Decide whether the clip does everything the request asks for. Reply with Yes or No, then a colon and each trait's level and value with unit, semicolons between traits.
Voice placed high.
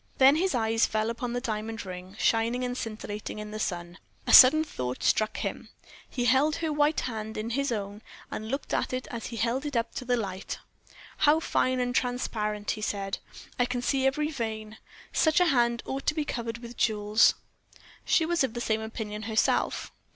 Yes: high, 235 Hz